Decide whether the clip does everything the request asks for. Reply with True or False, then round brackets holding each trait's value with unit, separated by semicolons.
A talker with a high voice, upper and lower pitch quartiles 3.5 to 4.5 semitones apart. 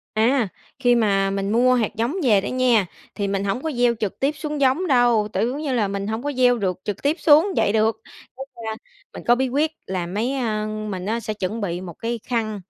True (225 Hz; 4.0 semitones)